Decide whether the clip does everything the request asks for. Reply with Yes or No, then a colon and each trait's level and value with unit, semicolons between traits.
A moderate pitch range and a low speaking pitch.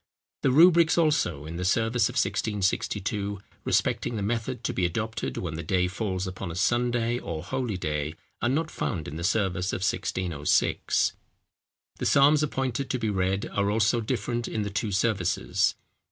Yes: average, 4.7 semitones; low, 105 Hz